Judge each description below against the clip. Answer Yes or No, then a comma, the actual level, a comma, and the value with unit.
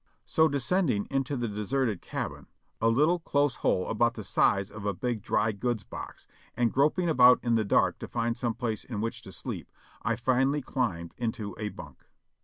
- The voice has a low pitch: Yes, low, 120 Hz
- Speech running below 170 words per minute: No, average, 195 wpm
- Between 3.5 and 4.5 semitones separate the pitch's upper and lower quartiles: Yes, average, 3.9 semitones